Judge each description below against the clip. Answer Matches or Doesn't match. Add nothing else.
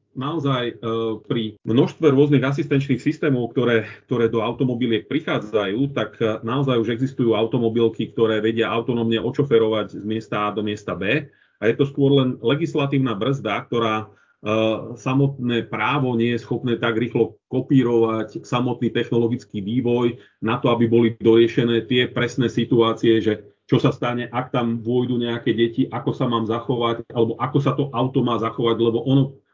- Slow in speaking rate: Doesn't match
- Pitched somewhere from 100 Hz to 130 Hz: Matches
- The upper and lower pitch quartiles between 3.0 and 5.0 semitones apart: Doesn't match